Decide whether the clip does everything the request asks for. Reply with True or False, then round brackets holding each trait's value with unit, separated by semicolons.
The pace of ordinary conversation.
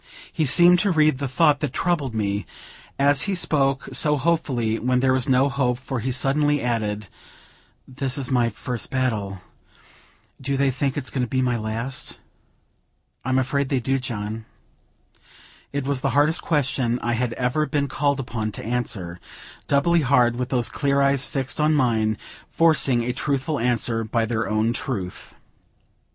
True (165 wpm)